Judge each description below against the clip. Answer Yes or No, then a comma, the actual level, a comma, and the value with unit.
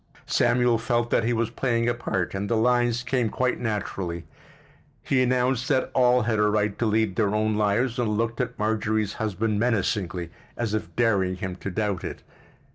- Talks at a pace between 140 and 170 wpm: No, average, 185 wpm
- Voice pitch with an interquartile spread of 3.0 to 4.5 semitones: No, narrow, 2.6 semitones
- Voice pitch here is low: Yes, low, 110 Hz